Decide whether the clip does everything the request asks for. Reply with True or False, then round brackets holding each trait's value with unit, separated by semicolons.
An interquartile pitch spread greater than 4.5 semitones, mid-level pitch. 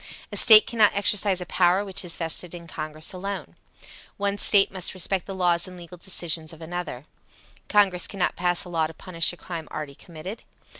False (2.6 semitones; 180 Hz)